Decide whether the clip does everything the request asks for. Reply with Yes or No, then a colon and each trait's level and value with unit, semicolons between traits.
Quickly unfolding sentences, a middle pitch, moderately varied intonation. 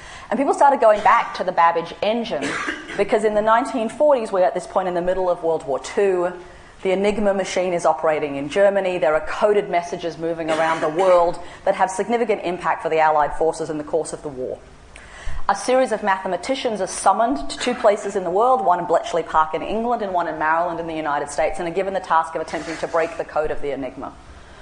Yes: fast, 225 wpm; medium, 175 Hz; average, 4.0 semitones